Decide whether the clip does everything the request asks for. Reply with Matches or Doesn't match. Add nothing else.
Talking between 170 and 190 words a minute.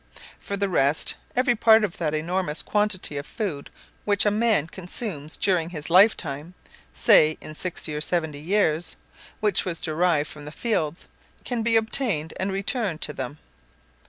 Doesn't match